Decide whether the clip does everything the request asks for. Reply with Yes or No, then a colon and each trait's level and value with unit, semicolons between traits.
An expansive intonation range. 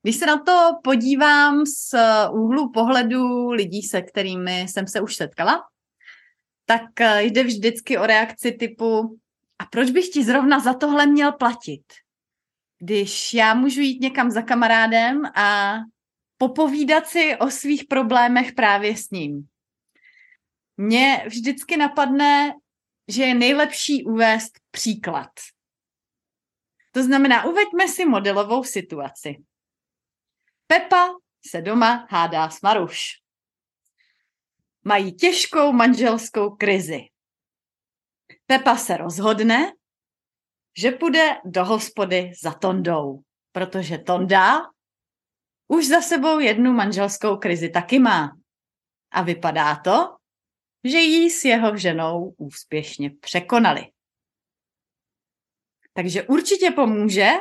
Yes: wide, 6.3 semitones